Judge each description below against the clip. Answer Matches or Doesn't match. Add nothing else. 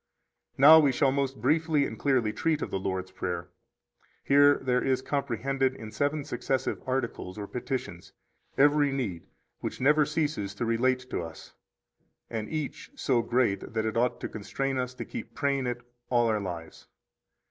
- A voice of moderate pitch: Doesn't match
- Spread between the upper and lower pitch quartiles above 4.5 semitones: Doesn't match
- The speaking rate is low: Doesn't match